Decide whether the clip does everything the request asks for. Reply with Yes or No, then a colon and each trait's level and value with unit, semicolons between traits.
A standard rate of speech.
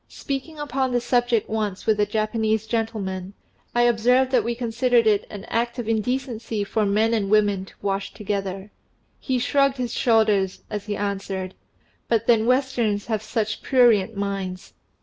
Yes: average, 160 wpm